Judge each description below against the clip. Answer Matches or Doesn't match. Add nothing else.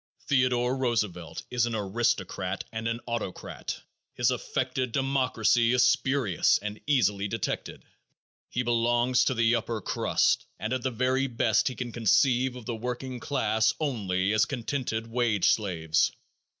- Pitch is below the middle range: Matches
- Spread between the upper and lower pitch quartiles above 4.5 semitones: Doesn't match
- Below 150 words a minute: Matches